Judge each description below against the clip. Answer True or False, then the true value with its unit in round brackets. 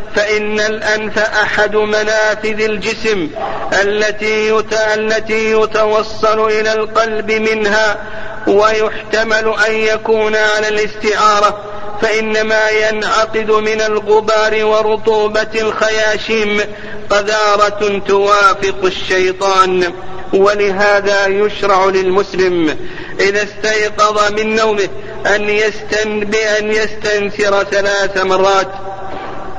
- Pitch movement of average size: False (1.0 semitones)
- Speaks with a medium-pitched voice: False (215 Hz)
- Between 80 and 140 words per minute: False (70 wpm)